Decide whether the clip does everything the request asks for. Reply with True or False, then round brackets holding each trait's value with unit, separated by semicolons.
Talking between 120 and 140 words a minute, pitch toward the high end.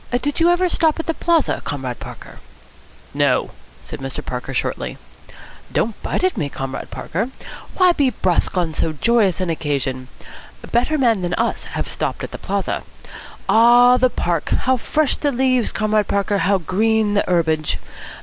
False (165 wpm; 215 Hz)